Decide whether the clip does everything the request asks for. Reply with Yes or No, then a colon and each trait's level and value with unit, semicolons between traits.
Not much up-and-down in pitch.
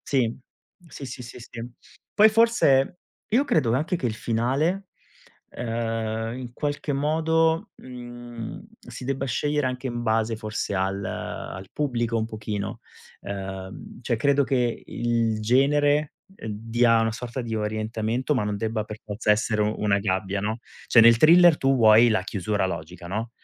No: average, 3.9 semitones